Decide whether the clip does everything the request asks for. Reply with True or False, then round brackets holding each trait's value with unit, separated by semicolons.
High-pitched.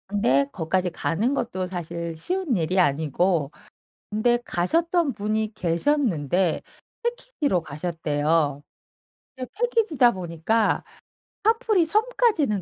True (195 Hz)